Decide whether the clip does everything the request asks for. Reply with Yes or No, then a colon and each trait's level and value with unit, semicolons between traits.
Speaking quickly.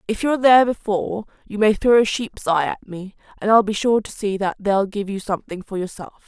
Yes: fast, 240 wpm